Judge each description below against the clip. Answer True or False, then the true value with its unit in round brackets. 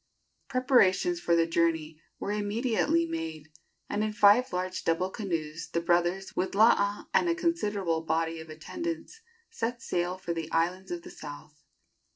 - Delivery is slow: False (155 wpm)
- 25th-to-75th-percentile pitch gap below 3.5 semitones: False (4.7 semitones)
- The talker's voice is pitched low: False (180 Hz)